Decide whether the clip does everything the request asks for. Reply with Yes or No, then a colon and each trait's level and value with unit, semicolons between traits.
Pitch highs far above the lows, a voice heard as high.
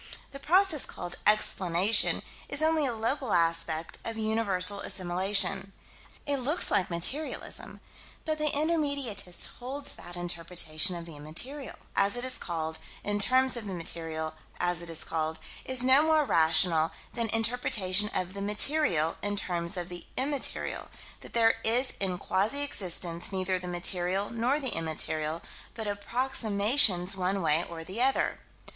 Yes: wide, 6.5 semitones; high, 200 Hz